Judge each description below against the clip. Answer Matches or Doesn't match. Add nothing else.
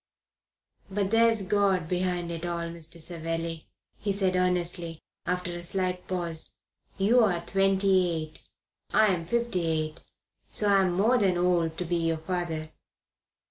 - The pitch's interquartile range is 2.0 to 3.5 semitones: Matches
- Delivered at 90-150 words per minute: Matches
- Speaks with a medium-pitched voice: Matches